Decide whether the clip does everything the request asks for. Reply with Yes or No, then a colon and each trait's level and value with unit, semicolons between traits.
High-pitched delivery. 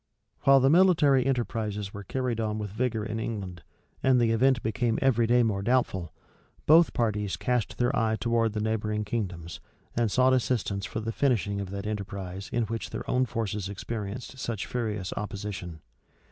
No: low, 110 Hz